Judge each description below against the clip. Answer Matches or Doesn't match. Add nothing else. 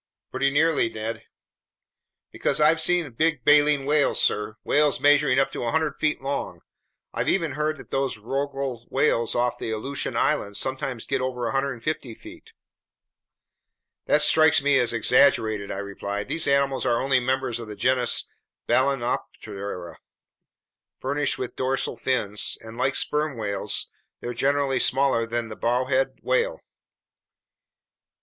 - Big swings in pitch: Doesn't match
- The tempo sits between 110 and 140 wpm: Matches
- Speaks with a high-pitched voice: Doesn't match